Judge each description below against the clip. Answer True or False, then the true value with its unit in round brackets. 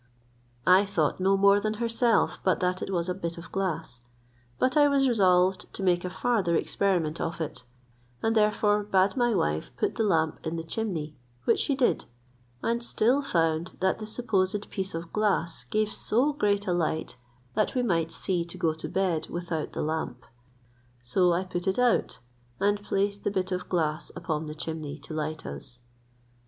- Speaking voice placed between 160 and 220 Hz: True (185 Hz)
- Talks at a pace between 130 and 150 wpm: False (185 wpm)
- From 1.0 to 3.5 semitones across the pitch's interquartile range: False (4.3 semitones)